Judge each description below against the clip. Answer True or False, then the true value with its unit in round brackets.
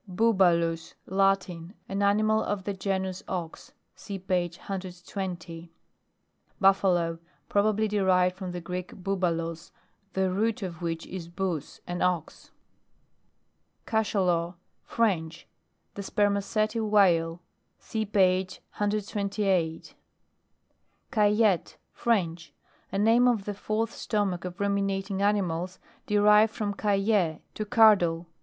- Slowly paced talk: True (110 wpm)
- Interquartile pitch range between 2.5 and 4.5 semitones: True (2.9 semitones)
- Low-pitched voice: False (195 Hz)